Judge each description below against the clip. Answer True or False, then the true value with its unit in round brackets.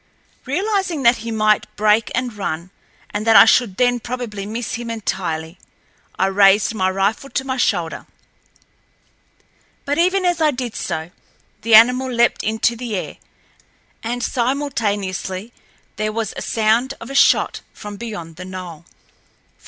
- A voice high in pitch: True (225 Hz)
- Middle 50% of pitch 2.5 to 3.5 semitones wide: False (4.3 semitones)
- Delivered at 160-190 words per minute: False (145 wpm)